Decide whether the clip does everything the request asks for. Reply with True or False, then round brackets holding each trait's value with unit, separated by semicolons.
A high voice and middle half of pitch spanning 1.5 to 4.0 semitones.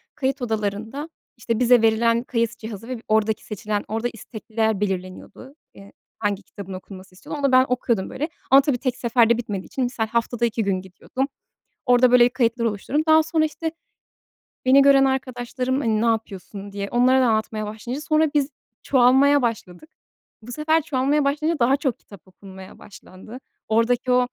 True (235 Hz; 3.6 semitones)